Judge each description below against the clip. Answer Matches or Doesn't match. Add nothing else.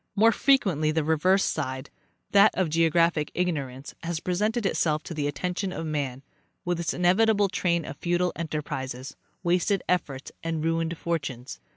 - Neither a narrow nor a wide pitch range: Matches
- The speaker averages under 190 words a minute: Matches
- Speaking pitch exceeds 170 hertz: Doesn't match